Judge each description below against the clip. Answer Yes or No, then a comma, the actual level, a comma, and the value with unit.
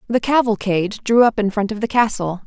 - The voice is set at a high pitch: Yes, high, 215 Hz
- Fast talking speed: Yes, fast, 220 wpm